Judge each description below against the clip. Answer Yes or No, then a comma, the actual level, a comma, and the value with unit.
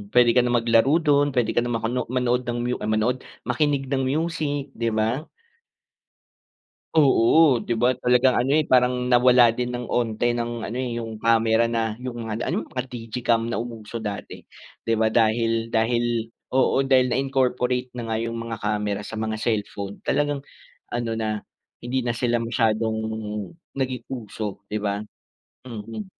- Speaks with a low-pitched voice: Yes, low, 120 Hz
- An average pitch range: No, narrow, 2.0 semitones